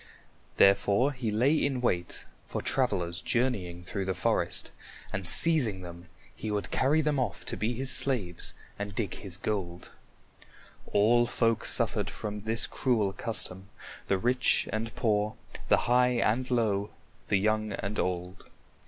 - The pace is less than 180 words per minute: Yes, average, 145 wpm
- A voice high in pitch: No, low, 110 Hz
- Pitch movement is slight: No, average, 4.2 semitones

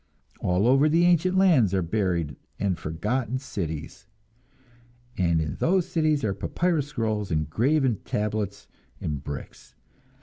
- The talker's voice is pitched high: No, low, 105 Hz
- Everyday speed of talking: No, slow, 130 wpm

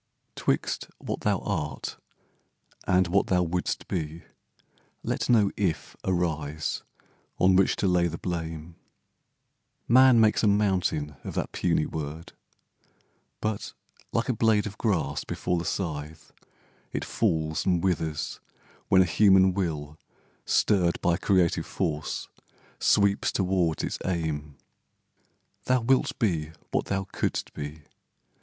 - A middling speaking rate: No, slow, 125 wpm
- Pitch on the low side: Yes, very low, 90 Hz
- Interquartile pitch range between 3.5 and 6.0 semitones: Yes, average, 4.0 semitones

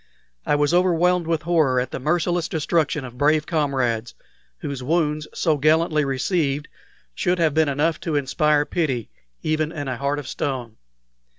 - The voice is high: No, medium, 150 Hz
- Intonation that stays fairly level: No, average, 3.0 semitones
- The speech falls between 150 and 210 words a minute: Yes, average, 160 wpm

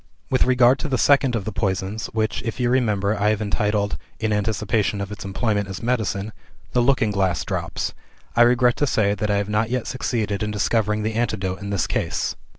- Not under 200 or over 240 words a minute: Yes, fast, 205 wpm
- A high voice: No, low, 105 Hz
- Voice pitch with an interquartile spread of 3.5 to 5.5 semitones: No, average, 2.9 semitones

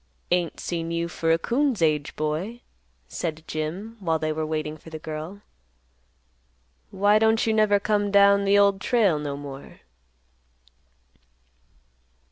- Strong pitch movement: No, average, 4.7 semitones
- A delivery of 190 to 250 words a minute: No, slow, 135 wpm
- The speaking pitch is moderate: Yes, medium, 170 Hz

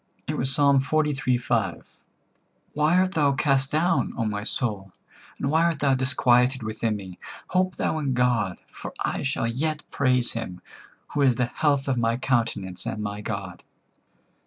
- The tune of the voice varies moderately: Yes, average, 4.2 semitones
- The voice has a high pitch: No, low, 130 Hz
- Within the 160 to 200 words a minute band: Yes, average, 165 wpm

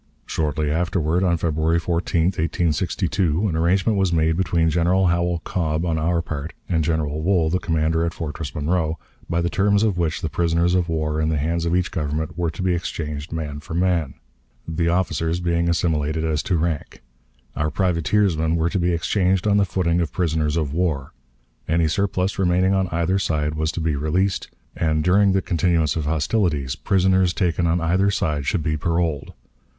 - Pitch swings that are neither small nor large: No, narrow, 2.3 semitones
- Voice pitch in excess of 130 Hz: No, very low, 85 Hz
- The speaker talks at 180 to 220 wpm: Yes, average, 185 wpm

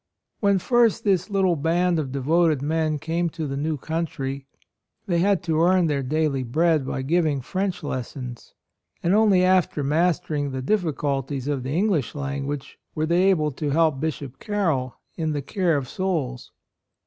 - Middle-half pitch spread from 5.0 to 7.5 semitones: No, average, 4.1 semitones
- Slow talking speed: No, average, 165 wpm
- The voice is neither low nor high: Yes, medium, 155 Hz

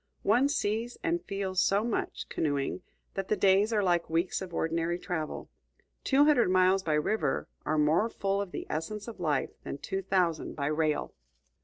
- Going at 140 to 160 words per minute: No, average, 175 wpm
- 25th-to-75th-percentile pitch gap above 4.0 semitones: Yes, average, 4.5 semitones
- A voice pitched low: No, medium, 185 Hz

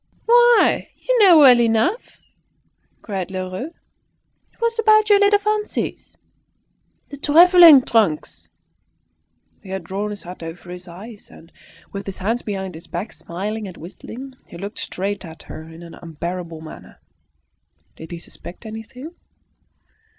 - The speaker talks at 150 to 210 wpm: No, average, 140 wpm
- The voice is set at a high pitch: Yes, high, 205 Hz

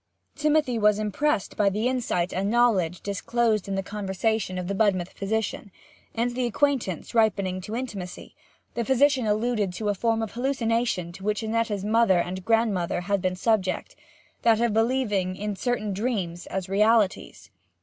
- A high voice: Yes, high, 210 Hz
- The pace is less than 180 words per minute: Yes, average, 160 wpm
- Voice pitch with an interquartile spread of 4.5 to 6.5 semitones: No, average, 3.5 semitones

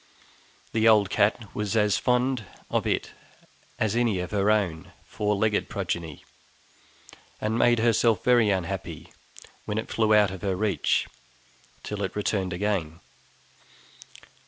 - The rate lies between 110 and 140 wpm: Yes, slow, 135 wpm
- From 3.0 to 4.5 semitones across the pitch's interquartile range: No, narrow, 2.5 semitones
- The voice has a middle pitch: No, low, 105 Hz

